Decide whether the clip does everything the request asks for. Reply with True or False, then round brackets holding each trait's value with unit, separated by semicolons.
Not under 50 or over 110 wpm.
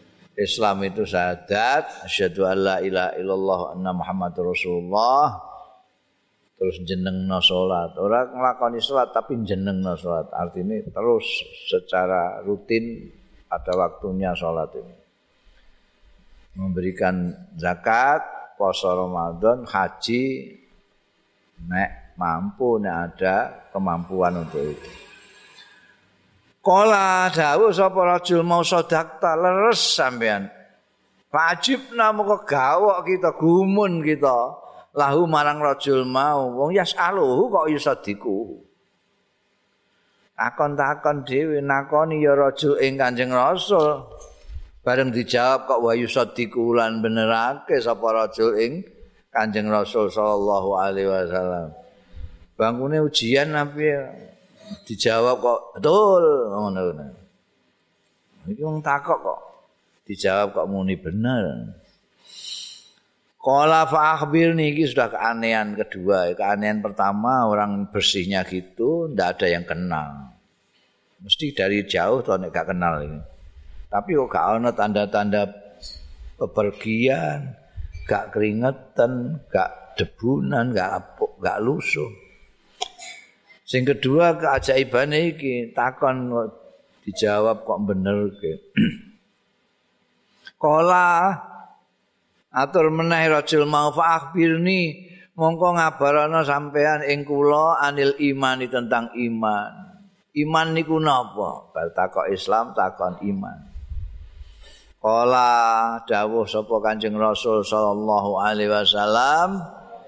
True (95 wpm)